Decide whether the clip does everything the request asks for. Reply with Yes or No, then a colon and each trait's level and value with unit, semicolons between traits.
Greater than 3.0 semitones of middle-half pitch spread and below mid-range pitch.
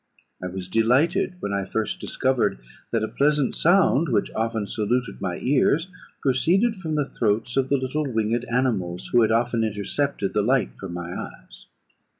Yes: average, 5.1 semitones; low, 120 Hz